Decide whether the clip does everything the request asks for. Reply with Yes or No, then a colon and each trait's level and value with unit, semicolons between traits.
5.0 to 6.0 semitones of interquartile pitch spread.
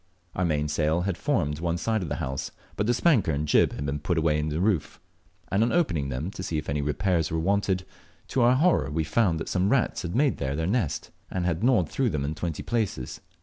Yes: wide, 5.4 semitones